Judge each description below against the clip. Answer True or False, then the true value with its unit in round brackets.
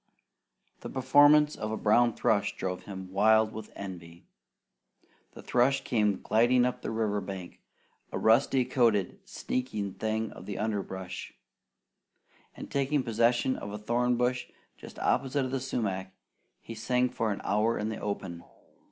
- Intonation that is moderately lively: True (3.6 semitones)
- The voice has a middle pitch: False (110 Hz)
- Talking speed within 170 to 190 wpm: False (145 wpm)